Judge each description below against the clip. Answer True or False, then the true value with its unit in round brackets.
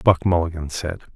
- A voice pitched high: False (85 Hz)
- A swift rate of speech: False (155 wpm)